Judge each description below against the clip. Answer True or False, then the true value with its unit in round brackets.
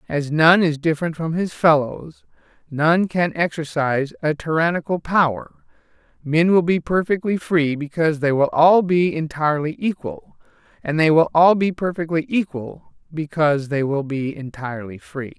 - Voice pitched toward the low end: False (160 Hz)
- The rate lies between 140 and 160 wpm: True (150 wpm)